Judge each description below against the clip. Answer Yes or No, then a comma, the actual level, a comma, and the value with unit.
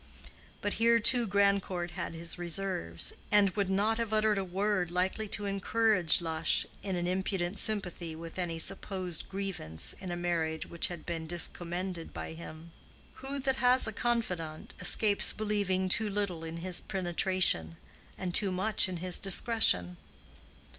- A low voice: No, medium, 185 Hz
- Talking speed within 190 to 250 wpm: No, average, 155 wpm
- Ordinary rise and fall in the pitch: Yes, average, 3.2 semitones